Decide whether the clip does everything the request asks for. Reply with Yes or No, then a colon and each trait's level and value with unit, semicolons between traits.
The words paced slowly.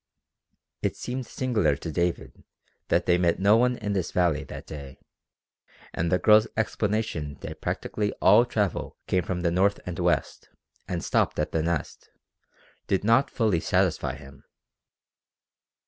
No: average, 145 wpm